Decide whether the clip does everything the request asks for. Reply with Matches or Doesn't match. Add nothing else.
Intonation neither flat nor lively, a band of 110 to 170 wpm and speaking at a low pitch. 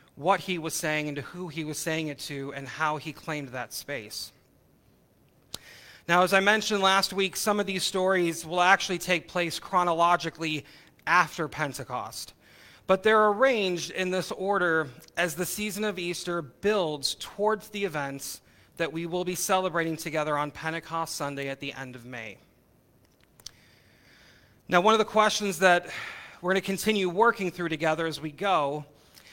Doesn't match